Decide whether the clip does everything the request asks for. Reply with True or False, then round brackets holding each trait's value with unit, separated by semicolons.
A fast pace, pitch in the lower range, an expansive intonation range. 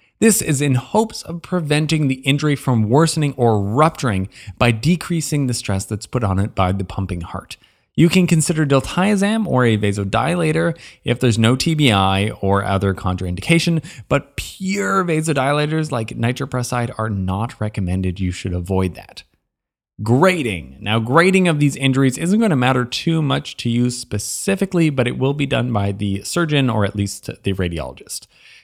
False (165 wpm; 125 Hz; 7.6 semitones)